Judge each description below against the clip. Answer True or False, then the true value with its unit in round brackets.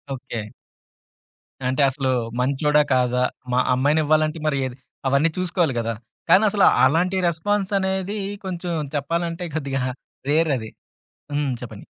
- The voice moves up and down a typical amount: True (4.8 semitones)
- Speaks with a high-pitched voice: False (150 Hz)